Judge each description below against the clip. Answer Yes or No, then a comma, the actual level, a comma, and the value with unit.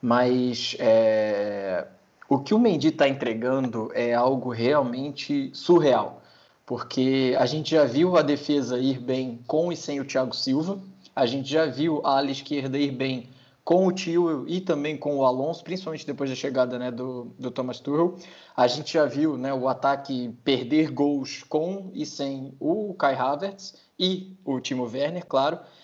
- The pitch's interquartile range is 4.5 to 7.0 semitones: No, average, 3.9 semitones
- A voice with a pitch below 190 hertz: Yes, medium, 140 Hz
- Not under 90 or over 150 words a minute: No, average, 170 wpm